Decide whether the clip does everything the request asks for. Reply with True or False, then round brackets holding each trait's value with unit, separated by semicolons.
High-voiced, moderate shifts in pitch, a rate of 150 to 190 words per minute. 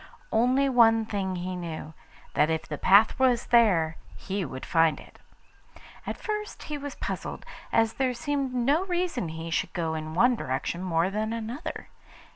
False (220 Hz; 7.4 semitones; 165 wpm)